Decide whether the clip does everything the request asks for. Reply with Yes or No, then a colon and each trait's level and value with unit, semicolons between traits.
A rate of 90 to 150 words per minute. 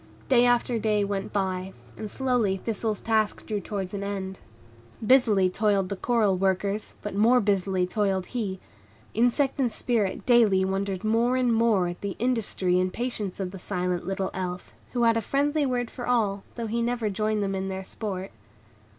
No: average, 175 wpm